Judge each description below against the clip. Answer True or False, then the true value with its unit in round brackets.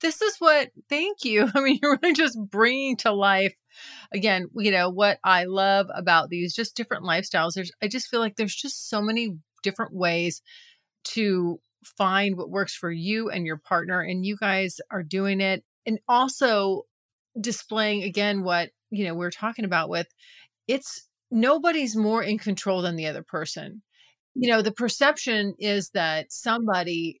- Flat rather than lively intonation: False (3.9 semitones)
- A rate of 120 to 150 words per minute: False (170 wpm)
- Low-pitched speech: False (205 Hz)